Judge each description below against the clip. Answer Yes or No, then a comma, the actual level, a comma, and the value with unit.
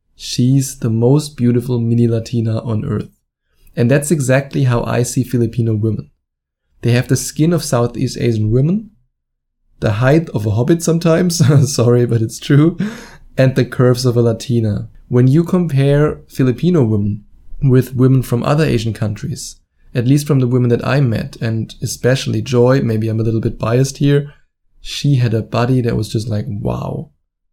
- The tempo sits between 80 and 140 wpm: No, average, 170 wpm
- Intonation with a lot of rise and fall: No, average, 3.6 semitones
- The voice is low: Yes, low, 125 Hz